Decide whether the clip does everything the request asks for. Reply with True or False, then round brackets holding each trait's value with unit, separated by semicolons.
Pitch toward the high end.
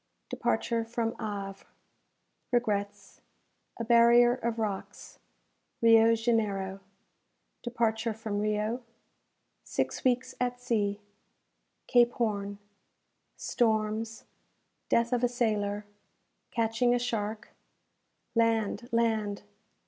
True (225 Hz)